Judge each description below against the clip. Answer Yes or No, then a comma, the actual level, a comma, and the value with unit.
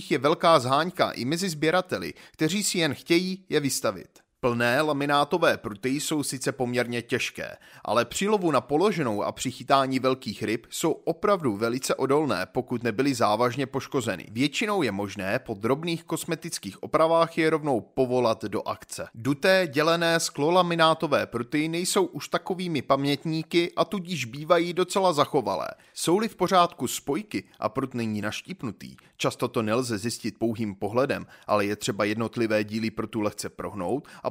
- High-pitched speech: No, medium, 140 Hz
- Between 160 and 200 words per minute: No, average, 145 wpm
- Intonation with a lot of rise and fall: Yes, wide, 5.8 semitones